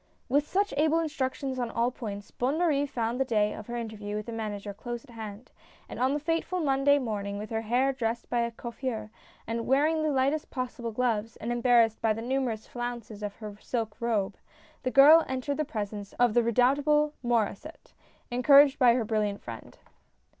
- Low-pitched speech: No, high, 240 Hz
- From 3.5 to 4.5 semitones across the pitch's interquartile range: Yes, average, 3.8 semitones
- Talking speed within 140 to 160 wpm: No, average, 190 wpm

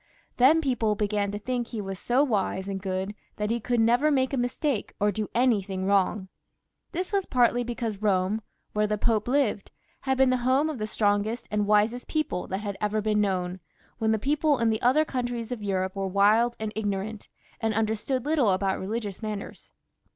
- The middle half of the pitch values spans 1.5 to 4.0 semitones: Yes, average, 3.4 semitones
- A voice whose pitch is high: Yes, high, 220 Hz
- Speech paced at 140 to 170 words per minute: No, average, 195 wpm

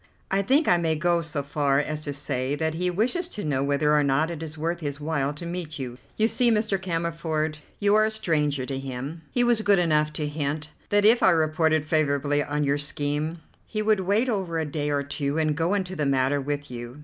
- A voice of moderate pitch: Yes, medium, 155 Hz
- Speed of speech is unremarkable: No, fast, 230 wpm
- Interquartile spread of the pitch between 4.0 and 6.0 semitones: No, average, 3.6 semitones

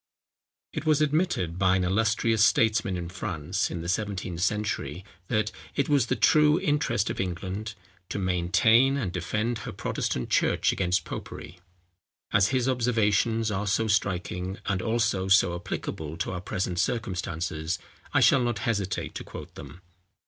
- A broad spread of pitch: No, average, 4.1 semitones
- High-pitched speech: No, low, 100 Hz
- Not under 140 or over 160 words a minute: Yes, average, 150 wpm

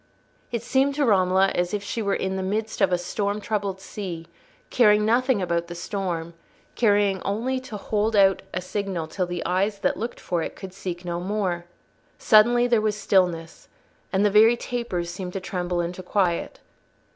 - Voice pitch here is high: Yes, high, 195 Hz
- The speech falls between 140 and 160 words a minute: No, average, 185 wpm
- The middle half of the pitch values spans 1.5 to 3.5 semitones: Yes, average, 3.1 semitones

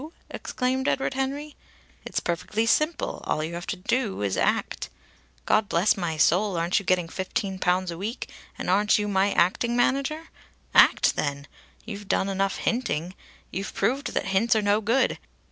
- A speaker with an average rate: Yes, average, 170 wpm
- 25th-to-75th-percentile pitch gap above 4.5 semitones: Yes, average, 5.2 semitones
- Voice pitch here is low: No, high, 200 Hz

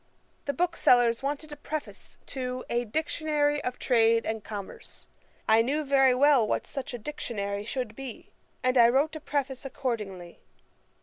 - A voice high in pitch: Yes, very high, 255 Hz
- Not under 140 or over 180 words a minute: Yes, average, 150 wpm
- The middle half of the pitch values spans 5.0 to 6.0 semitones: No, average, 4.1 semitones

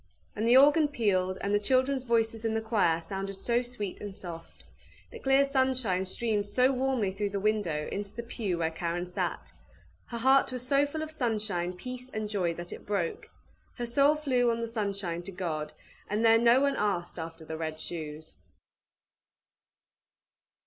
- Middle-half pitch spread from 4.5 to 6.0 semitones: Yes, wide, 5.6 semitones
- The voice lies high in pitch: Yes, high, 215 Hz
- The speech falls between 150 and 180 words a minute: Yes, average, 175 wpm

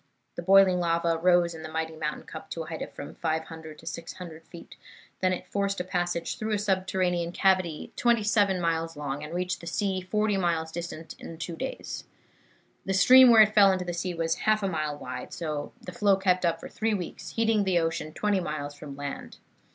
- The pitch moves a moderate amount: Yes, average, 3.2 semitones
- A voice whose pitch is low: No, medium, 175 Hz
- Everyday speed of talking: No, fast, 210 wpm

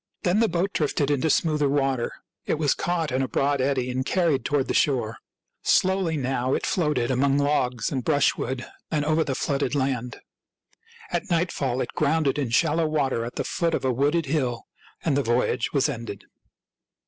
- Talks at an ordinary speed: Yes, average, 185 wpm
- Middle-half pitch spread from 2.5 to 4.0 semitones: Yes, average, 3.3 semitones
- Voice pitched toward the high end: No, medium, 140 Hz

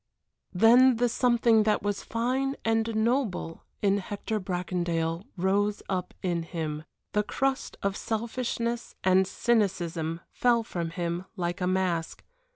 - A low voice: No, high, 200 Hz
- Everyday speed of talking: No, slow, 130 wpm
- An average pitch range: Yes, average, 4.7 semitones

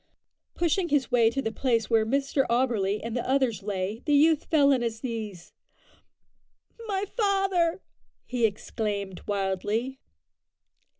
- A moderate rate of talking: No, slow, 130 wpm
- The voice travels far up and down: No, average, 4.9 semitones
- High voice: Yes, high, 240 Hz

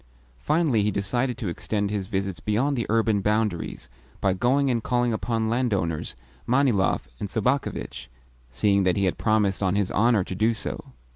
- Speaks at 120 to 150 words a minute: No, average, 165 wpm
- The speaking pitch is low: Yes, low, 105 Hz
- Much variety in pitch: No, average, 3.8 semitones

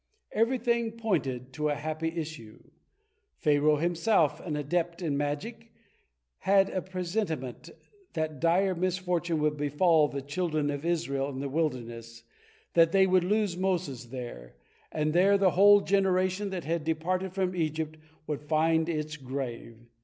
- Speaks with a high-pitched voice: No, medium, 160 Hz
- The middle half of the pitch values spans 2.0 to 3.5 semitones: No, average, 4.1 semitones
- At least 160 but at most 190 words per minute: No, average, 140 wpm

